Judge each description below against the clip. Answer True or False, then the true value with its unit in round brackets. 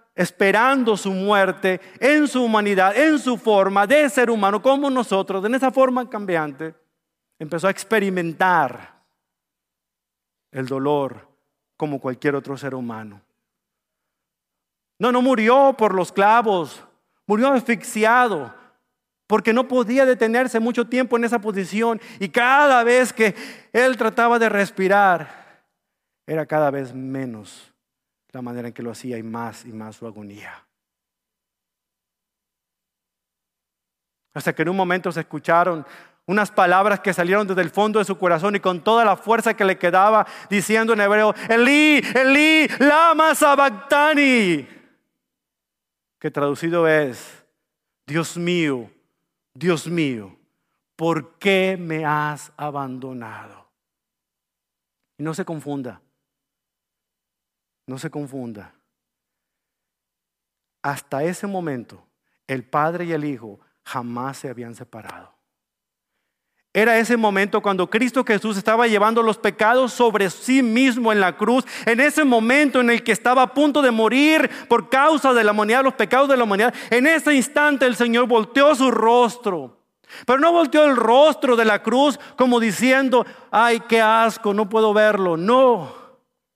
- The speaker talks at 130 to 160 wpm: True (135 wpm)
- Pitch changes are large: True (7.3 semitones)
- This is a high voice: True (215 Hz)